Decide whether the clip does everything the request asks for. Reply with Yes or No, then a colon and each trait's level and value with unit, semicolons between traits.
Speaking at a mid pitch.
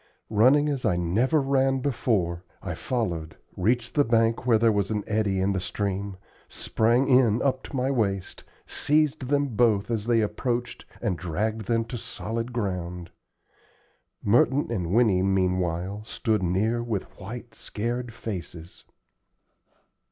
No: low, 110 Hz